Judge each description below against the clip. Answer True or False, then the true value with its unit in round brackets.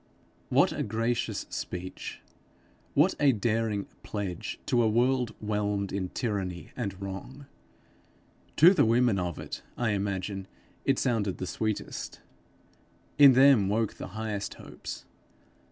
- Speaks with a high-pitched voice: False (105 Hz)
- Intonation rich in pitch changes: False (3.7 semitones)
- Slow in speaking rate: True (125 wpm)